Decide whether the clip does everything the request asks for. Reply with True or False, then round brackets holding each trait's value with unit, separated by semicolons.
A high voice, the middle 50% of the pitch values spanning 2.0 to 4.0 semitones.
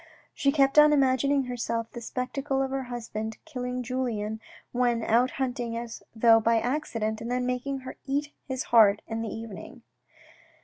True (245 Hz; 2.7 semitones)